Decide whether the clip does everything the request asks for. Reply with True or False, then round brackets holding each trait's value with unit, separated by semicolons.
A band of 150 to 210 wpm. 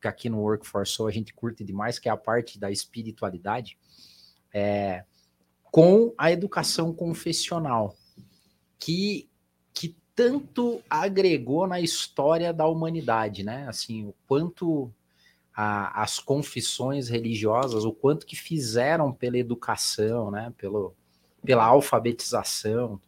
False (120 wpm)